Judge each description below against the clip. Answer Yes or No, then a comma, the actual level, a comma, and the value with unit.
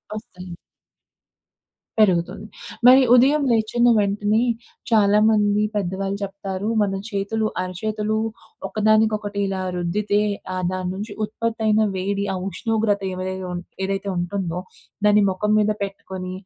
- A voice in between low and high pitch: No, high, 205 Hz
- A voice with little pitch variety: Yes, narrow, 2.2 semitones